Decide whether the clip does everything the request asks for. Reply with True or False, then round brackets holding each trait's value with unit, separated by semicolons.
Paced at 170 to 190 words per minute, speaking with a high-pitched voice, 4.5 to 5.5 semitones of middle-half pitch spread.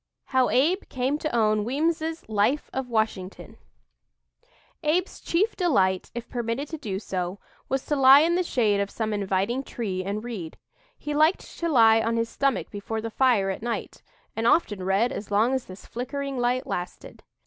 True (175 wpm; 240 Hz; 5.1 semitones)